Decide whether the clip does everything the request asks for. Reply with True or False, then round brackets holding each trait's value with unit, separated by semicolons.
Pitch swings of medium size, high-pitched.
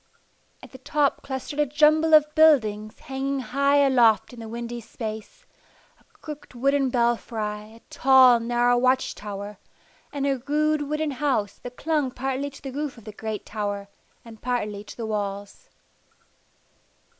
True (4.4 semitones; 255 Hz)